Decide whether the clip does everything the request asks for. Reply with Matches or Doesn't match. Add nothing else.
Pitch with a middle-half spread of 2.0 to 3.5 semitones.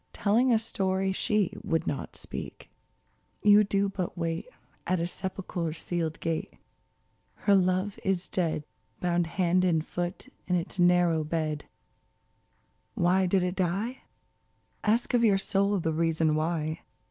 Matches